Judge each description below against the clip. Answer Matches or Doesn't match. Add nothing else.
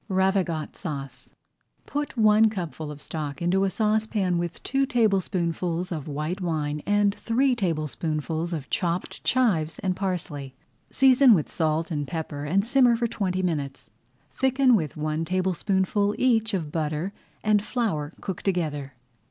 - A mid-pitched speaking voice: Matches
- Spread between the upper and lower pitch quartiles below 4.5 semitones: Doesn't match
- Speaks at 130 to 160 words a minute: Matches